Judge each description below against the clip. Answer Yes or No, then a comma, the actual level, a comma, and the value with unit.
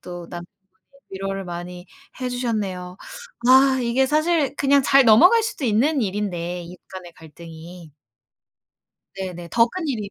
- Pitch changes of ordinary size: No, wide, 6.9 semitones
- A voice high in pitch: Yes, high, 200 Hz